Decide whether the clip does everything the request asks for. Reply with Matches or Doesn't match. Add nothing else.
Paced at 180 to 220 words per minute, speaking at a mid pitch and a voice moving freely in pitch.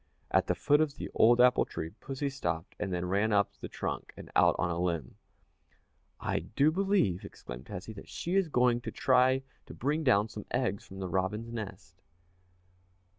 Doesn't match